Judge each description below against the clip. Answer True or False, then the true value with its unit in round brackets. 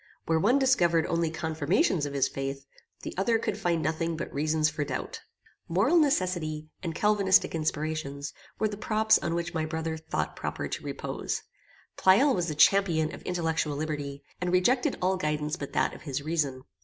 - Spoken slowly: False (175 wpm)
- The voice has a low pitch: False (160 Hz)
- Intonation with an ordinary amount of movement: True (3.6 semitones)